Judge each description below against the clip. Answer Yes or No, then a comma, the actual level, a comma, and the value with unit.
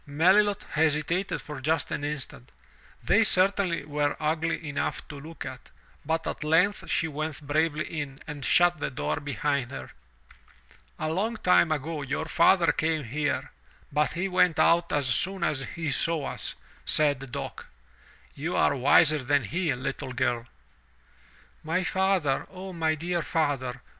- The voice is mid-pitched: Yes, medium, 155 Hz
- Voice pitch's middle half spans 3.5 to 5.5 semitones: No, average, 3.0 semitones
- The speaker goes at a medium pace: Yes, average, 160 wpm